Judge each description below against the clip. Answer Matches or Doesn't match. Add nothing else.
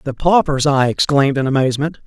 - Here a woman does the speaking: Doesn't match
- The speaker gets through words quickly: Doesn't match